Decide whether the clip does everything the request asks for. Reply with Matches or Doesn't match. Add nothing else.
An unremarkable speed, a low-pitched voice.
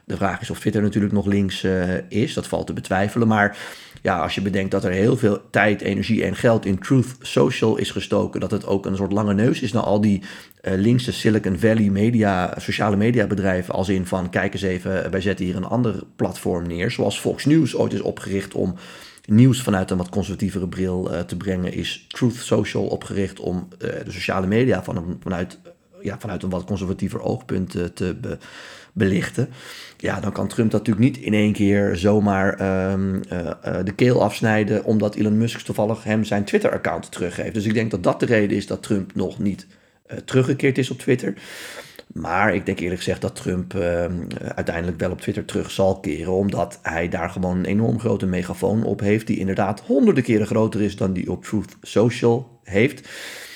Doesn't match